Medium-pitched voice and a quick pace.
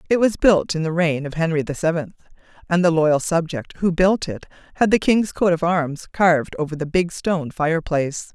Yes: medium, 170 Hz; fast, 210 wpm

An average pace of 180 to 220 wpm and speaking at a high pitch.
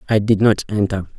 No: average, 200 wpm; low, 105 Hz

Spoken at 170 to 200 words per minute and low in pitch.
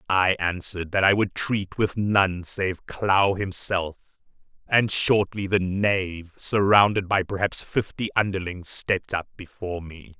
No: average, 140 wpm; very low, 95 Hz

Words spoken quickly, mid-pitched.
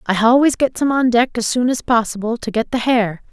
No: fast, 255 wpm; high, 235 Hz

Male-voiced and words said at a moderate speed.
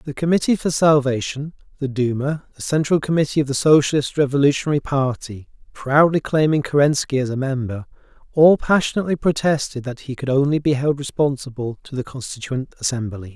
Yes: male; average, 145 wpm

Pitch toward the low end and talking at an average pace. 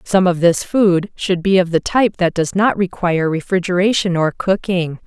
No: medium, 185 Hz; average, 190 wpm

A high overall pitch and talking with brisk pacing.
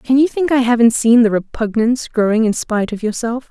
Yes: high, 235 Hz; fast, 225 wpm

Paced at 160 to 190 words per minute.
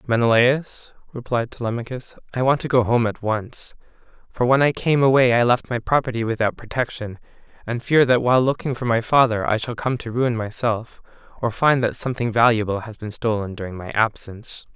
Yes: average, 185 wpm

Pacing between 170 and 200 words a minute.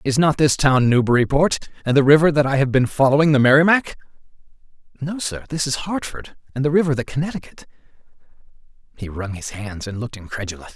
Yes: average, 180 wpm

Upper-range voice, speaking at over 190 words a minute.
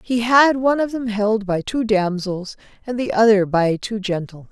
Yes: high, 215 Hz; average, 200 wpm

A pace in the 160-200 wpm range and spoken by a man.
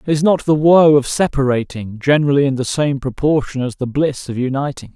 Yes: average, 195 wpm; male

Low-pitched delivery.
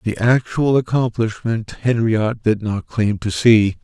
Yes: low, 110 Hz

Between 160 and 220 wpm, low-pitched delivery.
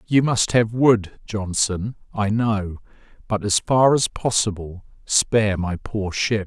No: average, 150 wpm; low, 105 Hz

